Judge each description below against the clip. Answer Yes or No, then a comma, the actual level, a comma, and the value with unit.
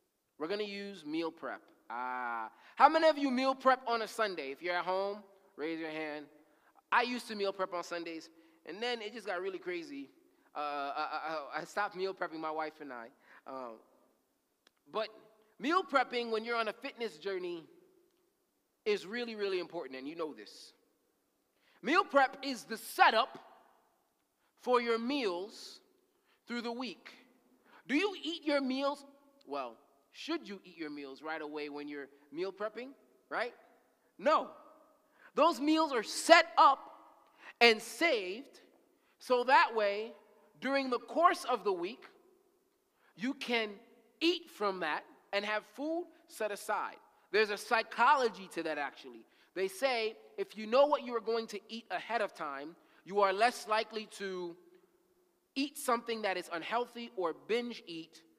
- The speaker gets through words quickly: No, average, 160 wpm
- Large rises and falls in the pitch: Yes, wide, 7.9 semitones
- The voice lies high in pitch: Yes, high, 225 Hz